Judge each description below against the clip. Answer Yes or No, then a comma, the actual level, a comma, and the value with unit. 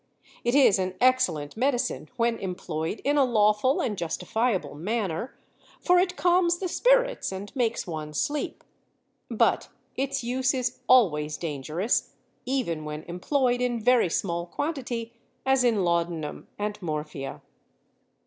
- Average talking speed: No, slow, 130 wpm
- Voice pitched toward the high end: Yes, high, 225 Hz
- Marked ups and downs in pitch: Yes, wide, 7.1 semitones